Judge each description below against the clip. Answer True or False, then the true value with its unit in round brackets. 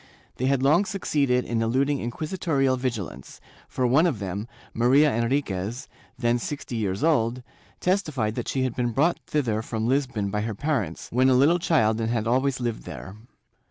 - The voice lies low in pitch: True (125 Hz)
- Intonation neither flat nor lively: True (3.9 semitones)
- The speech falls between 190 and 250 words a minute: False (170 wpm)